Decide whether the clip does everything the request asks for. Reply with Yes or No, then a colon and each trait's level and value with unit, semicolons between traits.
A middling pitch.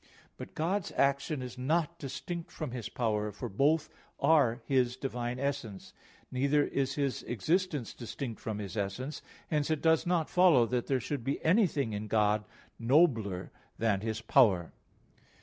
No: low, 130 Hz